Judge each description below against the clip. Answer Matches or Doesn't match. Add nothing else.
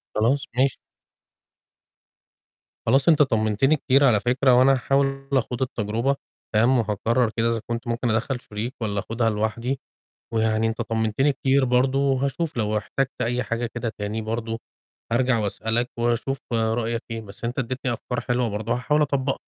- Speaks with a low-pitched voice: Matches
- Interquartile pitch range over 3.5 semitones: Doesn't match